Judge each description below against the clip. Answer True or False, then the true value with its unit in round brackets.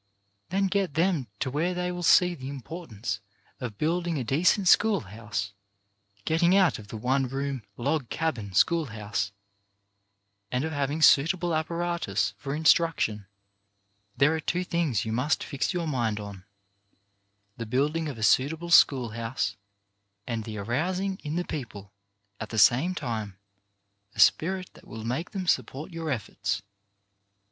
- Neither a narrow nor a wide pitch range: False (7.2 semitones)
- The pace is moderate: True (155 wpm)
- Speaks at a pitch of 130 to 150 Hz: True (140 Hz)